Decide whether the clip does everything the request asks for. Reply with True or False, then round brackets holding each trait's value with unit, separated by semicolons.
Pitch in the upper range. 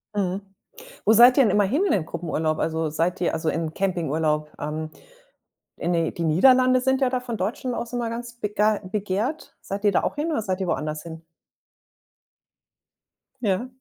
True (195 Hz)